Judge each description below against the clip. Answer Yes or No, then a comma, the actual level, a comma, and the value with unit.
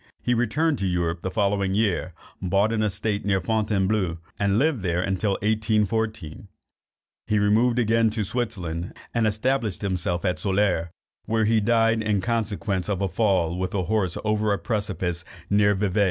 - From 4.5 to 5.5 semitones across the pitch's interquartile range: No, average, 2.9 semitones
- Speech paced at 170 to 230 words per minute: No, average, 160 wpm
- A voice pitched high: No, low, 105 Hz